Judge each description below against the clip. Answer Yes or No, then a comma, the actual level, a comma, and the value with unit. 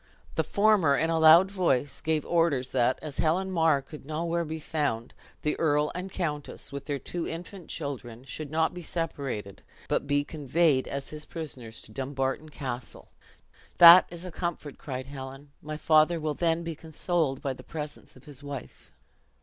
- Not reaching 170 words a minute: No, average, 175 wpm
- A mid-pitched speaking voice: Yes, medium, 150 Hz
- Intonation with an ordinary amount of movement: Yes, average, 3.3 semitones